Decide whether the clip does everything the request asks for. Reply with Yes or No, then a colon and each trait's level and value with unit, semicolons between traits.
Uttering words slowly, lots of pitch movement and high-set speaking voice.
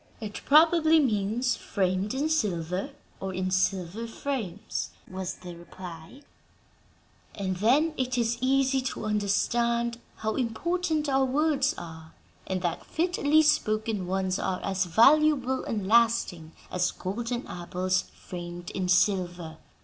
Yes: slow, 125 wpm; wide, 6.2 semitones; high, 215 Hz